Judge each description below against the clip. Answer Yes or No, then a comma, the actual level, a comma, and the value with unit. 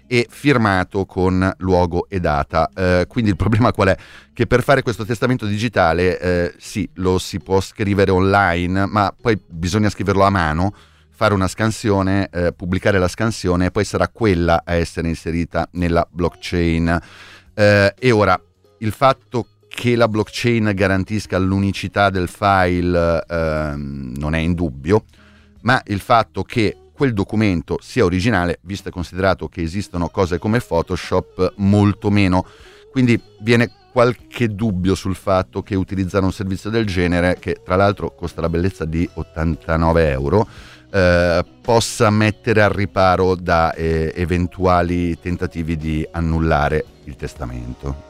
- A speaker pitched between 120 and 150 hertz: No, very low, 95 Hz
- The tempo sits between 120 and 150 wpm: Yes, average, 145 wpm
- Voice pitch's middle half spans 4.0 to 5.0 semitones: No, average, 3.5 semitones